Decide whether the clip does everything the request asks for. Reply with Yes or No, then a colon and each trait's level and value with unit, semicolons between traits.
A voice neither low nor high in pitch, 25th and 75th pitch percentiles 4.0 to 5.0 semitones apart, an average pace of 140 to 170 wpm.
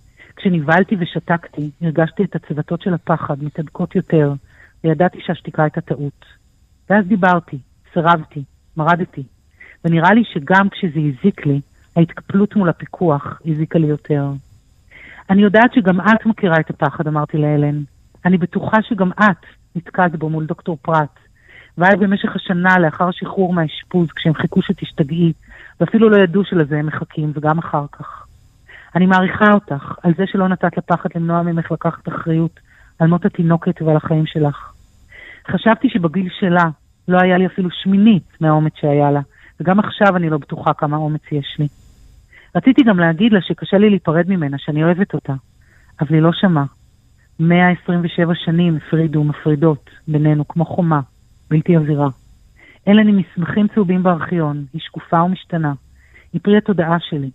No: medium, 165 Hz; average, 3.4 semitones; average, 145 wpm